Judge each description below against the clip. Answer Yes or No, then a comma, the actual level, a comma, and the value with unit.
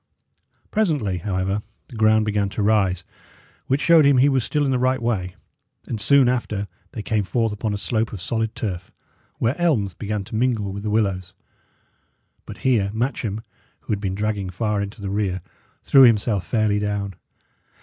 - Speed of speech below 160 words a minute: No, average, 175 wpm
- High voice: No, low, 105 Hz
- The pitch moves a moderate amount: Yes, average, 3.2 semitones